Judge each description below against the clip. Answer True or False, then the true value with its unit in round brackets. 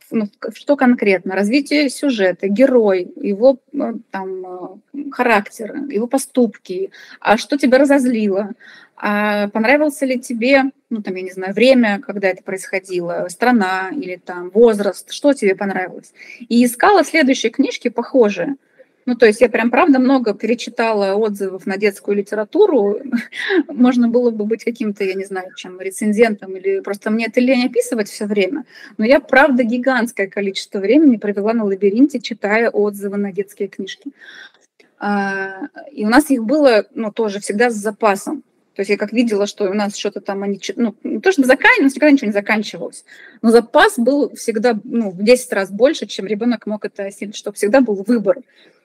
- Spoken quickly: True (165 wpm)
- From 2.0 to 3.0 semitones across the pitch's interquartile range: False (4.6 semitones)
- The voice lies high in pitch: True (225 Hz)